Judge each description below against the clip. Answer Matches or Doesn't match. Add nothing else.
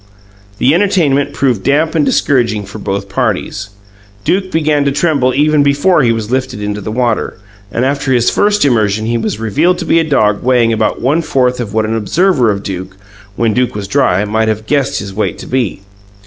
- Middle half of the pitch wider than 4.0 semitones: Matches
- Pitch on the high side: Doesn't match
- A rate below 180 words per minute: Doesn't match